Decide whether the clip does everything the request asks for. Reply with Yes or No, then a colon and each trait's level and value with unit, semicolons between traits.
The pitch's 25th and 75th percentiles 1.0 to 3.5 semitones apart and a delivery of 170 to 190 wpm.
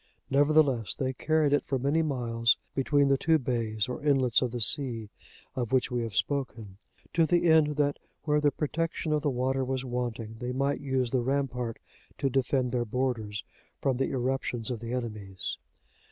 Yes: average, 3.1 semitones; average, 180 wpm